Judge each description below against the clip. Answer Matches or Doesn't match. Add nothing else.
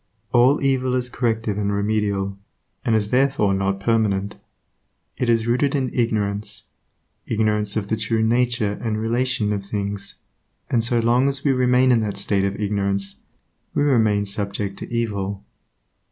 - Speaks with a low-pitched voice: Matches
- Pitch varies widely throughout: Doesn't match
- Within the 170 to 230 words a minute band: Doesn't match